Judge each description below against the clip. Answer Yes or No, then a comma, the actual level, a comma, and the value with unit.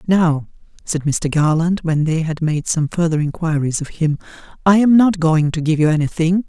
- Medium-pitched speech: Yes, medium, 160 Hz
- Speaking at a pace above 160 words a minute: Yes, average, 195 wpm